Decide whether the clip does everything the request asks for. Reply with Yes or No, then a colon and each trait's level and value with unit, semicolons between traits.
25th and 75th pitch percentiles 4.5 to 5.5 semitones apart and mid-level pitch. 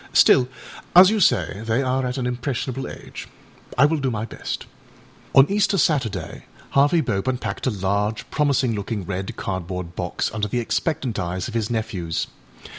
No: average, 5.2 semitones; low, 120 Hz